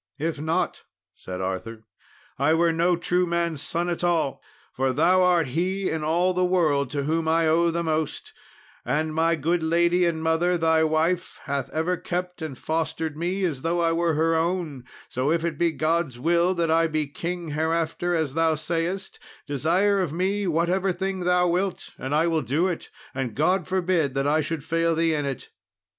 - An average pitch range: No, narrow, 2.2 semitones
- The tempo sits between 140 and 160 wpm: No, average, 190 wpm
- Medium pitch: Yes, medium, 165 Hz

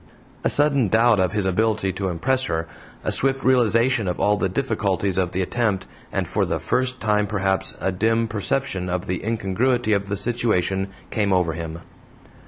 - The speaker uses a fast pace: No, average, 180 wpm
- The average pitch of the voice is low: Yes, low, 105 Hz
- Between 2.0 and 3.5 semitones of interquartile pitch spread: No, average, 3.9 semitones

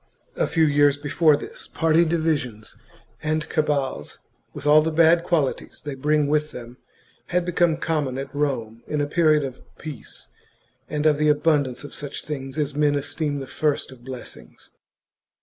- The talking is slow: No, average, 165 wpm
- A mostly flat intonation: Yes, narrow, 2.2 semitones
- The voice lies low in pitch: No, medium, 150 Hz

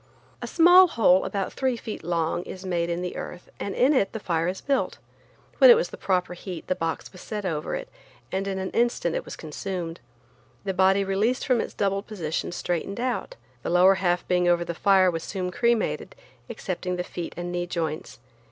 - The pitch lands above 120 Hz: Yes, medium, 185 Hz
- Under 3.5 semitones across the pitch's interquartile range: Yes, average, 2.8 semitones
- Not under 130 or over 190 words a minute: No, fast, 205 wpm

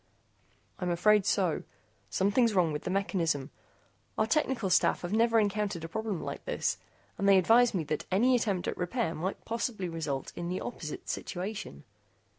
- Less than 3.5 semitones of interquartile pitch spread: No, average, 4.3 semitones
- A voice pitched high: Yes, high, 195 Hz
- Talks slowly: No, average, 165 wpm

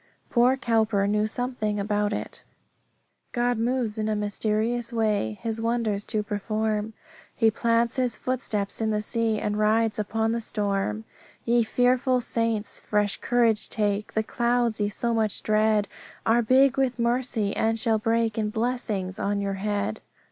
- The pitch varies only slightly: Yes, narrow, 2.1 semitones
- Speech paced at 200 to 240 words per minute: No, average, 155 wpm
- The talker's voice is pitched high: Yes, high, 220 Hz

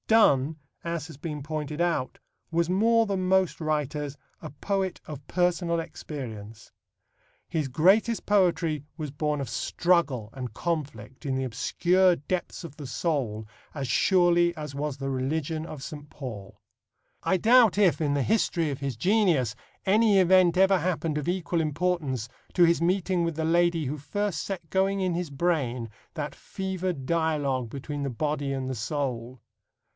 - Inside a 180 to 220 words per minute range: No, average, 160 wpm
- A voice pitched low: No, medium, 155 Hz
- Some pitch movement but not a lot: Yes, average, 4.5 semitones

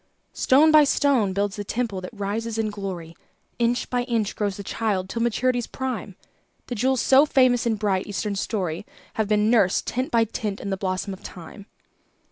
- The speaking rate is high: No, average, 185 wpm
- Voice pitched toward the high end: Yes, high, 215 Hz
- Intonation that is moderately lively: Yes, average, 3.7 semitones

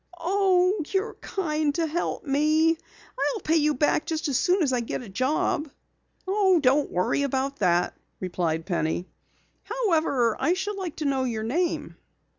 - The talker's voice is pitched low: No, very high, 305 Hz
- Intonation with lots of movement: Yes, wide, 5.8 semitones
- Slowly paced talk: No, average, 155 wpm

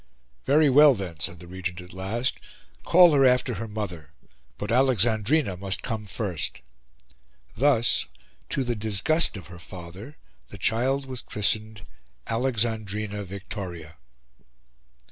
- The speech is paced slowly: Yes, slow, 125 wpm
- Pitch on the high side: No, low, 105 Hz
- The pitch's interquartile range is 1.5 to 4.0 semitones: No, average, 5.2 semitones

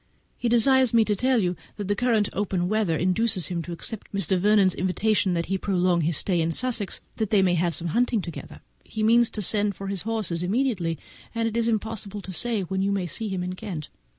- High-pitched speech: Yes, high, 200 Hz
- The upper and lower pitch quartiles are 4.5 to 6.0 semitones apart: No, average, 3.8 semitones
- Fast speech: Yes, fast, 220 wpm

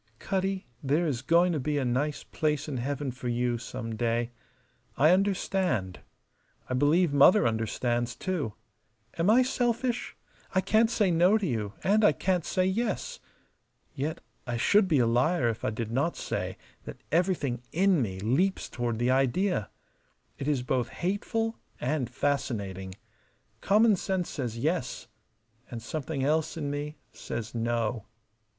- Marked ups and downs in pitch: Yes, wide, 7.5 semitones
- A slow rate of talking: No, average, 150 wpm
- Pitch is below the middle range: No, medium, 145 Hz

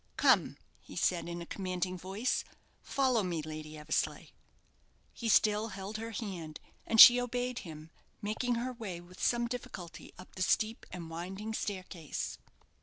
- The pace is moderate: Yes, average, 150 wpm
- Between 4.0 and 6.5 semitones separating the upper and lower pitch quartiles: Yes, average, 4.9 semitones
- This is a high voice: Yes, high, 195 Hz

